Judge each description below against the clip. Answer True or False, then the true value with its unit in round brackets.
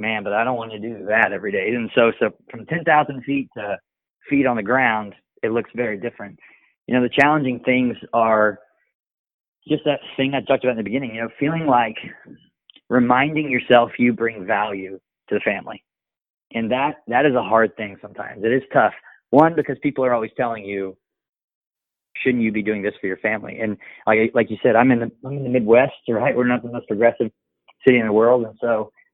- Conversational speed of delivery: False (210 wpm)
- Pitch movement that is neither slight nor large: True (3.2 semitones)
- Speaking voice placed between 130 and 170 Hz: False (120 Hz)